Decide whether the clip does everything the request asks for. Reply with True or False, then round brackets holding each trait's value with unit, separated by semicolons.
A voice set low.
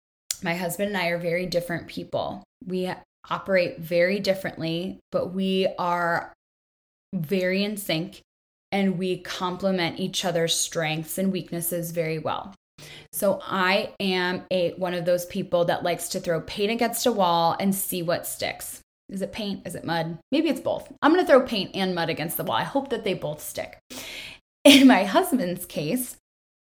False (185 Hz)